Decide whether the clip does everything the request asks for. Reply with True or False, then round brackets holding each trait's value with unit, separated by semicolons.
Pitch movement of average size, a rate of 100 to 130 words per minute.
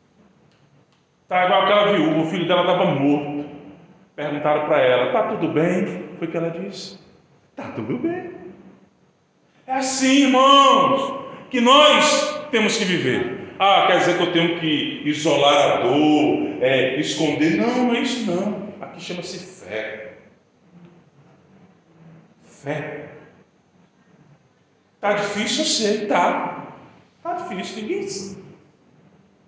False (7.4 semitones; 120 wpm)